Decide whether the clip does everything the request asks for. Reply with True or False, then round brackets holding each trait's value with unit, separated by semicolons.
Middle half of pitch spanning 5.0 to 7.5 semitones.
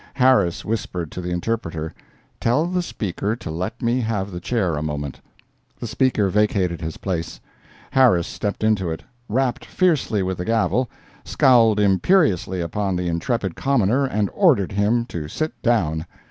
True (5.4 semitones)